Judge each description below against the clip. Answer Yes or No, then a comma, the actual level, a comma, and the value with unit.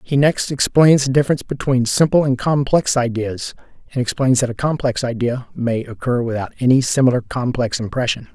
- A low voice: Yes, low, 125 Hz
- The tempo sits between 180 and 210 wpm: No, average, 165 wpm